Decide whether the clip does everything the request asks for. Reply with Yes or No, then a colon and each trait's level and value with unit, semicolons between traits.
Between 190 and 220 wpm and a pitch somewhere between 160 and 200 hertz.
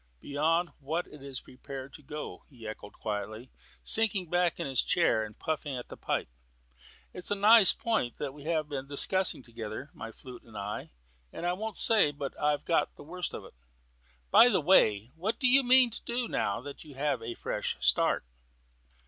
No: average, 195 wpm; medium, 150 Hz